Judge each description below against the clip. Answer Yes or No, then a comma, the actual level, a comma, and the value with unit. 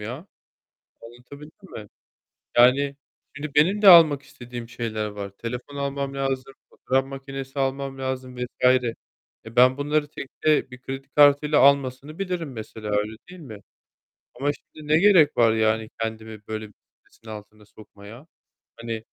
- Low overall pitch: Yes, low, 130 Hz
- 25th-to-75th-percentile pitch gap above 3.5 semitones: Yes, average, 4.1 semitones